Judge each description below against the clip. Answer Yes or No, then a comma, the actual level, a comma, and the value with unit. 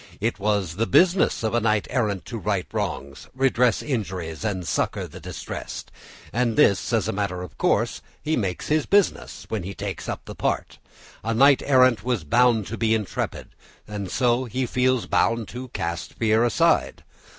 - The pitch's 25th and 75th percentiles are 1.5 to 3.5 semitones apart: No, average, 4.0 semitones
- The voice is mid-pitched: No, low, 110 Hz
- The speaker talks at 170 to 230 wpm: Yes, average, 175 wpm